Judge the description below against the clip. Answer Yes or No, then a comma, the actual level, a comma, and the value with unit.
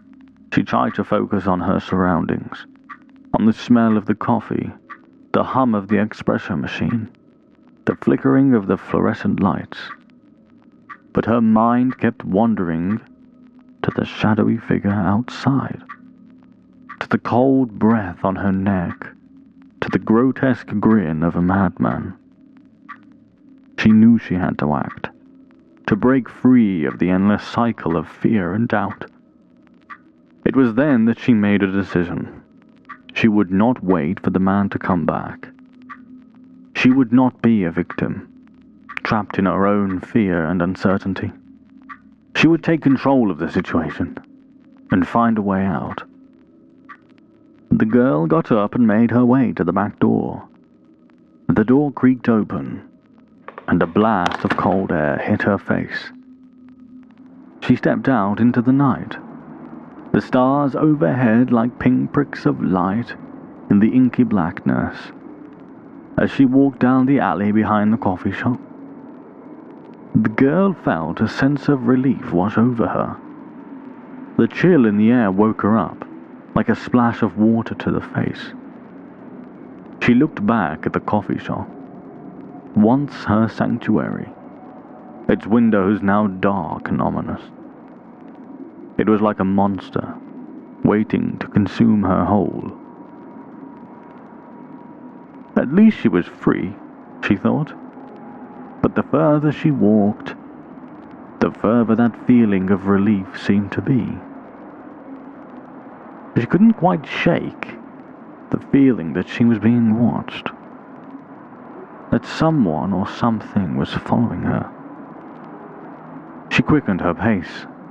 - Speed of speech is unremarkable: No, slow, 130 wpm